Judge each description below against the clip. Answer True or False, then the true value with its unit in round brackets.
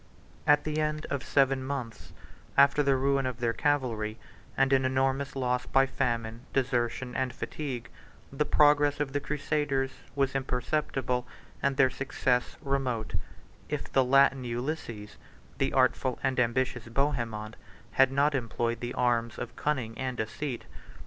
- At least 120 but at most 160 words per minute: True (140 wpm)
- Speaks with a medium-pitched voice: False (130 Hz)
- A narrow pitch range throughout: True (2.2 semitones)